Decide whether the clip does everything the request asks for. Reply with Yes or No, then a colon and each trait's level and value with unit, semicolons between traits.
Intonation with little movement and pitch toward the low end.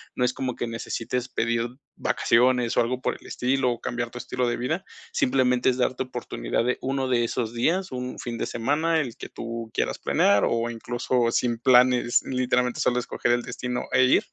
Yes: narrow, 1.3 semitones; low, 125 Hz